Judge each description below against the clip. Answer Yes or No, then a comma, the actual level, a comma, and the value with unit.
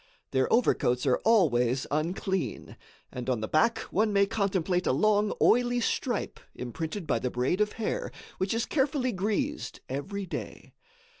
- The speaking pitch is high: Yes, high, 195 Hz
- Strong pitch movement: Yes, wide, 8.3 semitones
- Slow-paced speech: No, average, 150 wpm